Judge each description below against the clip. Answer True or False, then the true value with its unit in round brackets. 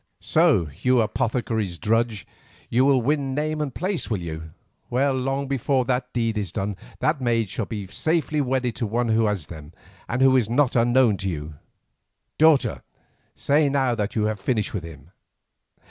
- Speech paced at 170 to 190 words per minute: True (175 wpm)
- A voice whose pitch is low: True (120 Hz)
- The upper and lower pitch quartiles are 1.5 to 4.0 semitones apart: False (4.5 semitones)